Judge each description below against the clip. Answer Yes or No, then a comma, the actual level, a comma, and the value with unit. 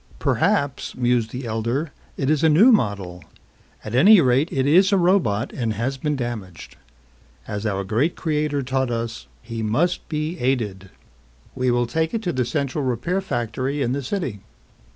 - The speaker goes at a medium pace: Yes, average, 170 wpm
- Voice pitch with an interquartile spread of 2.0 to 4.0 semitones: No, average, 4.9 semitones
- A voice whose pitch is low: Yes, low, 130 Hz